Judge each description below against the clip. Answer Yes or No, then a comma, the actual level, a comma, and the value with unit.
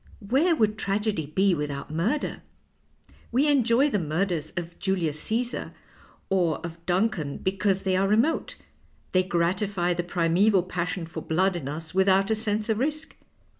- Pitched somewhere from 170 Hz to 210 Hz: Yes, high, 190 Hz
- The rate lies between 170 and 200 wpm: No, average, 155 wpm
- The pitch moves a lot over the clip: No, average, 4.2 semitones